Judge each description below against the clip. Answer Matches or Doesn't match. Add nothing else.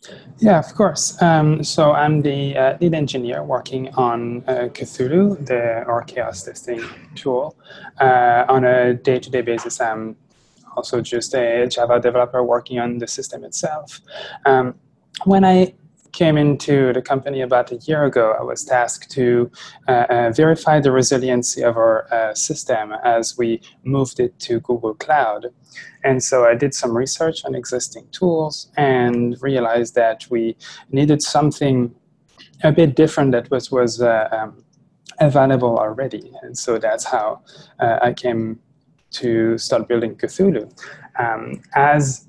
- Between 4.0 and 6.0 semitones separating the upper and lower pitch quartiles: Doesn't match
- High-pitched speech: Doesn't match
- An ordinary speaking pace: Matches